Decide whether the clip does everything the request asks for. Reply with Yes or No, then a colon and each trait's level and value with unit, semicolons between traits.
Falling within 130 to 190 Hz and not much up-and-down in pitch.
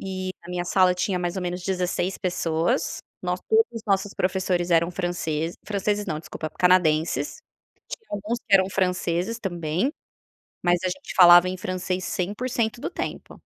Yes: medium, 185 Hz; narrow, 1.9 semitones